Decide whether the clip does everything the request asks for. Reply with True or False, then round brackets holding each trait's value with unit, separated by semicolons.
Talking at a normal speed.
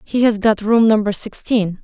True (195 wpm)